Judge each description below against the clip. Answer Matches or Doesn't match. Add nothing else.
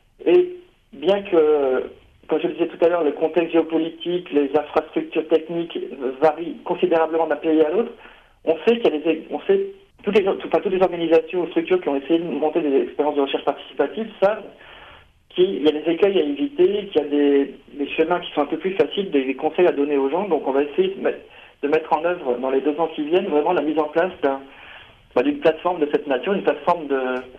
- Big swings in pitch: Doesn't match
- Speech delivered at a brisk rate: Matches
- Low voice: Doesn't match